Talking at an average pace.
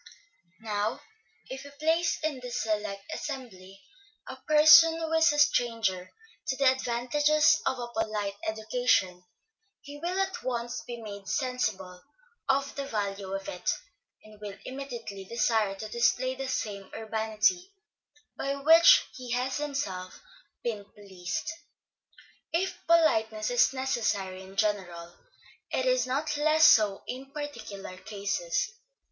No: slow, 130 wpm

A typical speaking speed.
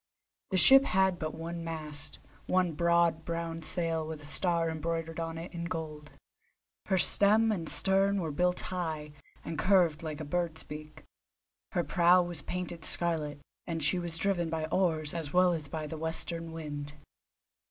Yes: average, 165 wpm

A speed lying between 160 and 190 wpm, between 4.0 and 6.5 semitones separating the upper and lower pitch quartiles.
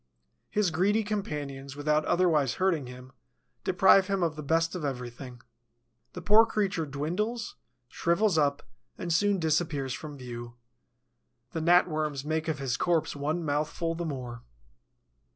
No: average, 140 wpm; average, 4.3 semitones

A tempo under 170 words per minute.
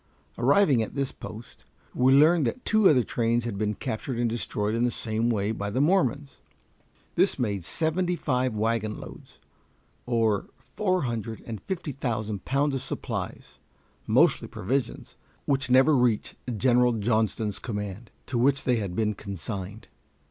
Yes: average, 150 wpm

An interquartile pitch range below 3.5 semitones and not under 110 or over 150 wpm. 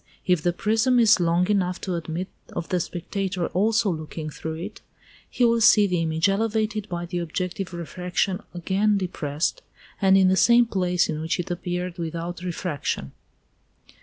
No: average, 2.8 semitones; average, 165 wpm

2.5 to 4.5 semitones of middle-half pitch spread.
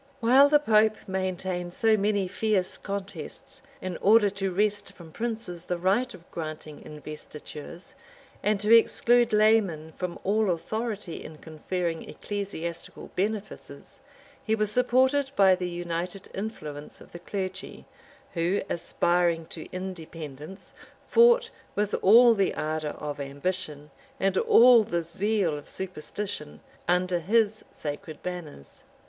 Yes: average, 4.2 semitones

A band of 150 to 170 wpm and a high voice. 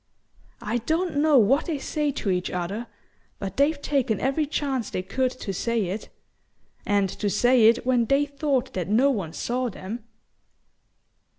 Yes: average, 165 wpm; high, 245 Hz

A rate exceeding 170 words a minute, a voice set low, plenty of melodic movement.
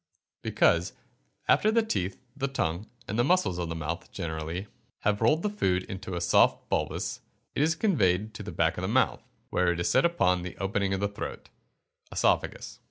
Yes: average, 195 wpm; low, 100 Hz; wide, 6.9 semitones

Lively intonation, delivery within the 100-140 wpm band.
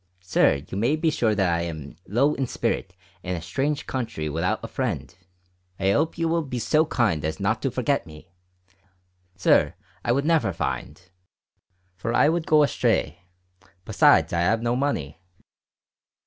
No: wide, 7.9 semitones; average, 165 wpm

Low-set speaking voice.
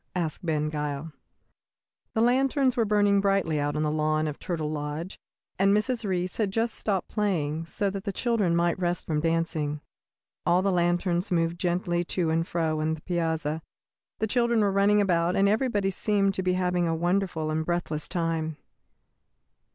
No: medium, 175 Hz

